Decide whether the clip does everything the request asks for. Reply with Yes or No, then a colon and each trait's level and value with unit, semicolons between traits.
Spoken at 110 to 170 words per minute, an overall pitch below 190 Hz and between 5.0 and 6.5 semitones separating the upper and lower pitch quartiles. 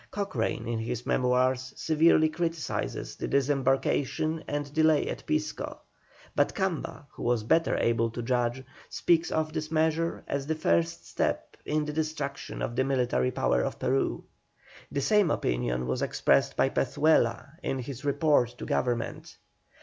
No: average, 150 wpm; medium, 140 Hz; average, 4.6 semitones